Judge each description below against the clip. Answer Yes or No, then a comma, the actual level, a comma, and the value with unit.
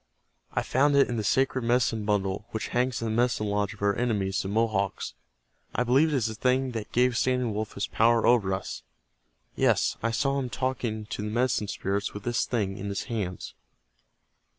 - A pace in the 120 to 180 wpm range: No, average, 195 wpm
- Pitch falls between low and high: No, low, 115 Hz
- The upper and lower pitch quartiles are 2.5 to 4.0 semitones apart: Yes, average, 3.4 semitones